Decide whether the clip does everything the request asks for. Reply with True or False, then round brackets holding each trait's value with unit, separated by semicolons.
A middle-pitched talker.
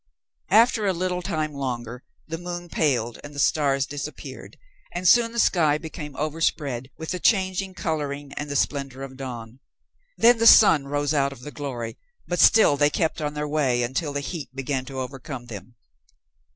True (145 Hz)